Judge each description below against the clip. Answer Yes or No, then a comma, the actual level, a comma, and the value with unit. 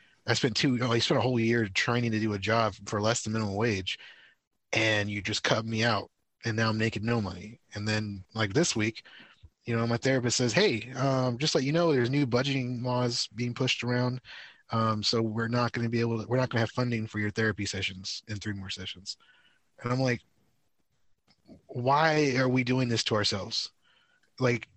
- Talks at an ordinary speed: No, fast, 215 wpm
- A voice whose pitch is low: Yes, low, 115 Hz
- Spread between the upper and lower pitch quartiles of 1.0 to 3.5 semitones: Yes, narrow, 2.5 semitones